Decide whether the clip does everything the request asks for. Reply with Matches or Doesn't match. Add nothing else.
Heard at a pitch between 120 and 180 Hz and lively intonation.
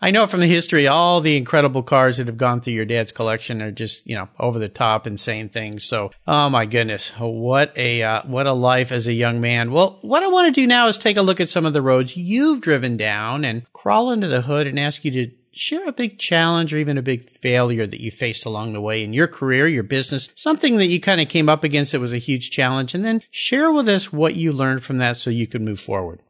Matches